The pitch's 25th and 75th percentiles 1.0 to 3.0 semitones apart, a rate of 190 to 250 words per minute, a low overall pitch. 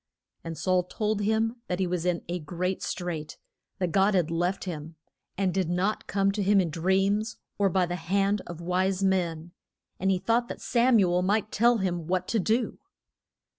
No: narrow, 2.5 semitones; average, 195 wpm; medium, 185 Hz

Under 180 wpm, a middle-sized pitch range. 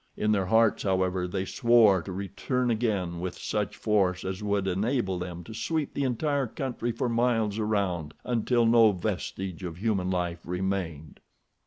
Yes: average, 160 wpm; average, 4.0 semitones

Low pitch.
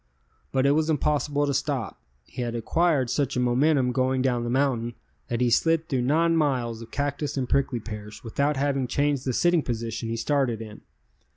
Yes: low, 130 Hz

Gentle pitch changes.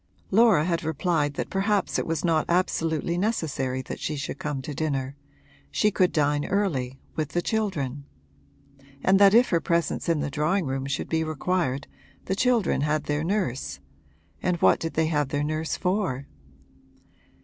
No: average, 4.3 semitones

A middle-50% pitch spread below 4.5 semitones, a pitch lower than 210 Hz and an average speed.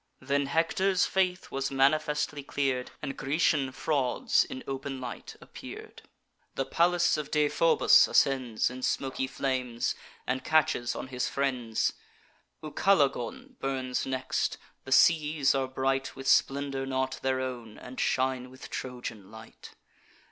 No: narrow, 2.4 semitones; low, 135 Hz; slow, 125 wpm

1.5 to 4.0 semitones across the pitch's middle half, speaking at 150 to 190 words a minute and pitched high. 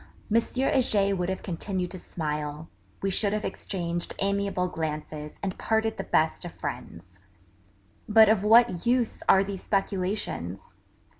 No: average, 3.7 semitones; slow, 135 wpm; high, 195 Hz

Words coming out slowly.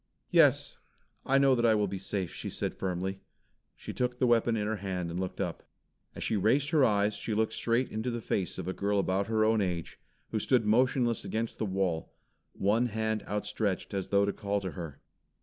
No: fast, 205 wpm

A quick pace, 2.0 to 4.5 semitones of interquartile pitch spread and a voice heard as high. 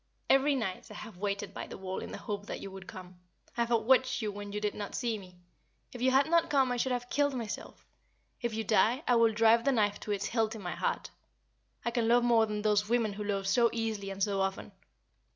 Yes: fast, 245 wpm; average, 3.0 semitones; high, 220 Hz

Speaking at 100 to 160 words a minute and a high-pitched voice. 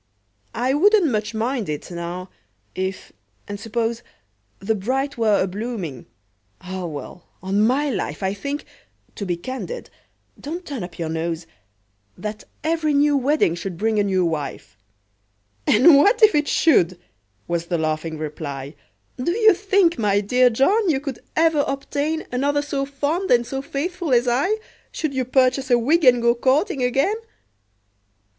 Yes: average, 145 wpm; high, 245 Hz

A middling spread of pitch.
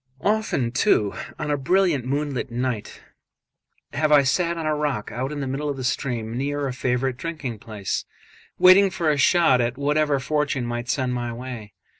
Yes: average, 3.5 semitones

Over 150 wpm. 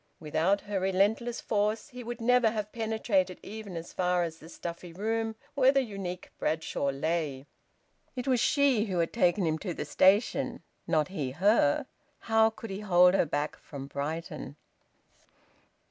Yes: average, 160 wpm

